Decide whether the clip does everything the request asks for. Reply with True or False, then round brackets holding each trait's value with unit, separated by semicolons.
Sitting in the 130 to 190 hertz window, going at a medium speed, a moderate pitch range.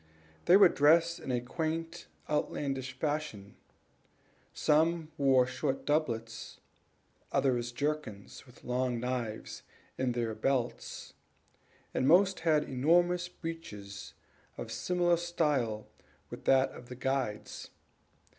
False (135 Hz; 115 wpm; 5.0 semitones)